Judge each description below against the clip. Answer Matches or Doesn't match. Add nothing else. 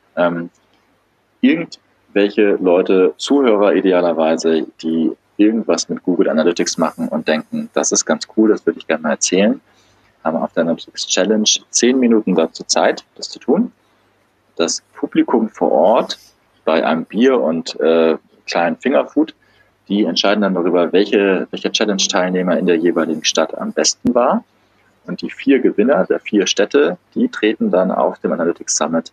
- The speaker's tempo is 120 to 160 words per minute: Matches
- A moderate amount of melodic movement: Matches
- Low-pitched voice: Matches